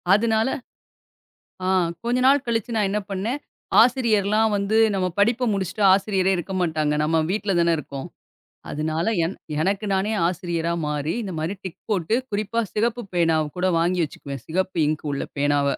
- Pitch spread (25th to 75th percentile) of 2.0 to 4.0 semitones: No, average, 4.7 semitones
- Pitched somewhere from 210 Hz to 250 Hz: No, high, 190 Hz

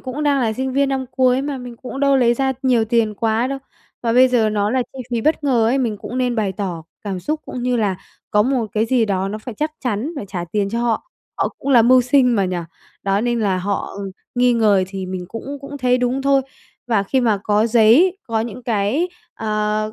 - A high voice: Yes, high, 235 Hz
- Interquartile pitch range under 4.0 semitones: Yes, average, 3.6 semitones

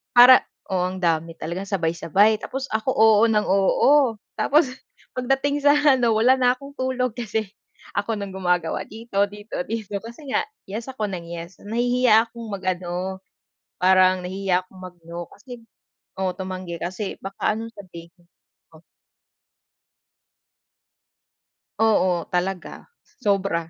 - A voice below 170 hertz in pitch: No, high, 200 Hz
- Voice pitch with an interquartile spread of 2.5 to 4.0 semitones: No, average, 4.5 semitones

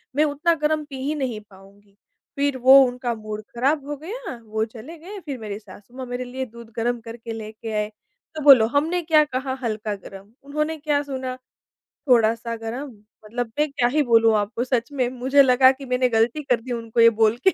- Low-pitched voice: No, high, 245 Hz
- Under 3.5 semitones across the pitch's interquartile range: No, average, 4.1 semitones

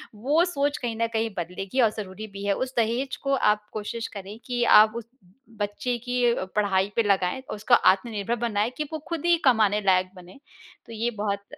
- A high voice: Yes, high, 220 Hz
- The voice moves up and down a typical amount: Yes, average, 3.4 semitones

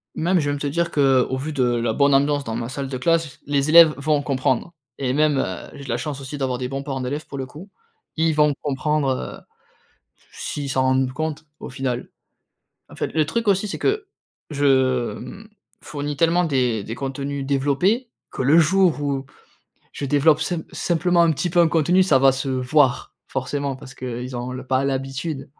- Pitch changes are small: No, average, 3.1 semitones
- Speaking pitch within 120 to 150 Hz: Yes, medium, 140 Hz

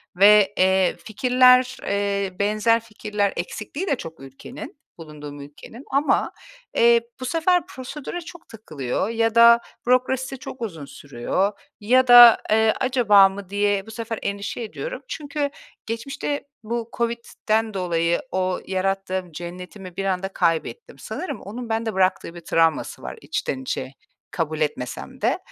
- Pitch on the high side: Yes, high, 210 Hz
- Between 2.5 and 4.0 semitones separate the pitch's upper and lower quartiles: No, average, 4.7 semitones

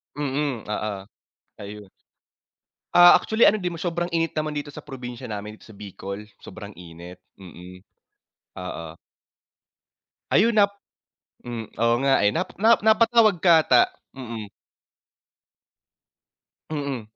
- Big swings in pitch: Yes, wide, 8.7 semitones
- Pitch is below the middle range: Yes, low, 125 Hz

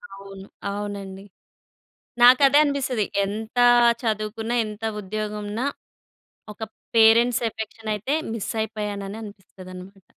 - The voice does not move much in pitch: Yes, narrow, 2.2 semitones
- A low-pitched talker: No, high, 215 Hz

